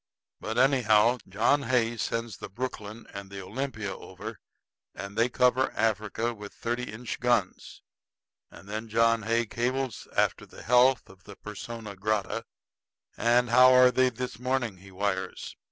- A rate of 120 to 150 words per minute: Yes, average, 145 wpm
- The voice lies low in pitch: Yes, low, 115 Hz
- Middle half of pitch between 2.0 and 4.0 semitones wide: Yes, average, 3.0 semitones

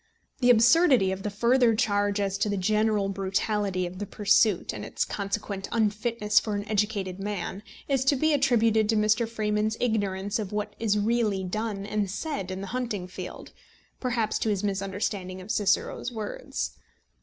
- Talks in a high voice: Yes, high, 210 Hz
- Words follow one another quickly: No, average, 165 wpm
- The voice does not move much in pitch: Yes, narrow, 2.3 semitones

